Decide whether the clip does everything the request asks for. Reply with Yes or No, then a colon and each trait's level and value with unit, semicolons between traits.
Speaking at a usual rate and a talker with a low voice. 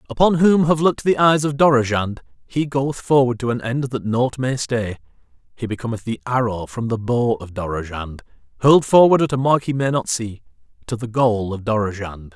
Yes: average, 195 wpm; low, 120 Hz